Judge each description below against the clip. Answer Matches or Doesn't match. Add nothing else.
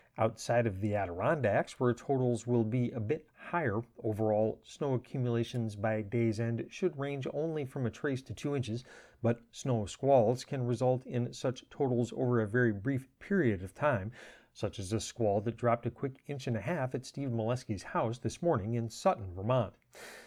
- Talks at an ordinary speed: Matches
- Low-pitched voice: Matches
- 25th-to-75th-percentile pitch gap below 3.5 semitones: Matches